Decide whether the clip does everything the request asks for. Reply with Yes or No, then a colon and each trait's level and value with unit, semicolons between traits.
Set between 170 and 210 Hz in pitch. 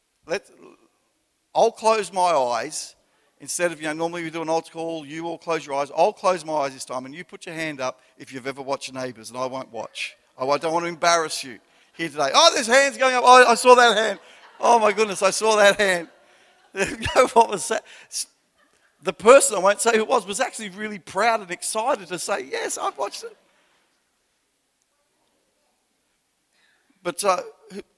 Yes: medium, 185 Hz